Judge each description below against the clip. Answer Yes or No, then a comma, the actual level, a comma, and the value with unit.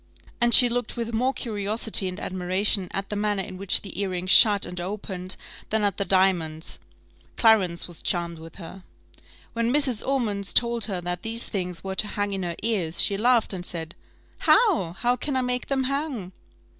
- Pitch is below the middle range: No, high, 200 Hz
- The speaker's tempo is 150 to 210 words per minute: Yes, average, 185 wpm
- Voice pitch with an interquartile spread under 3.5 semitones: No, average, 4.3 semitones